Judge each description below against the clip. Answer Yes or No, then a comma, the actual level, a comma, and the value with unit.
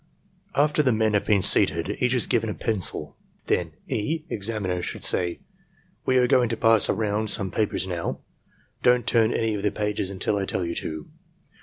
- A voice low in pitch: Yes, low, 105 Hz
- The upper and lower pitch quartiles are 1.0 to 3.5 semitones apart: Yes, average, 3.1 semitones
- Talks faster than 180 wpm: Yes, average, 190 wpm